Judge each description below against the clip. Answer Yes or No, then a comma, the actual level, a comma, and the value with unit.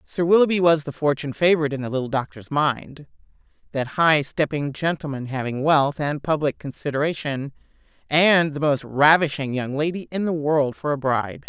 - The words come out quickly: No, average, 165 wpm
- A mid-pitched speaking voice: Yes, medium, 145 Hz